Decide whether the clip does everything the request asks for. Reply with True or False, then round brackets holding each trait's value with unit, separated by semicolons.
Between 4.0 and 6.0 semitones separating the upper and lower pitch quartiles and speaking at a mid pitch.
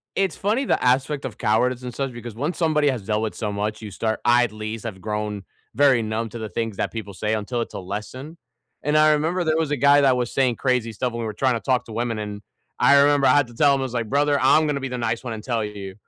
False (4.6 semitones; 120 Hz)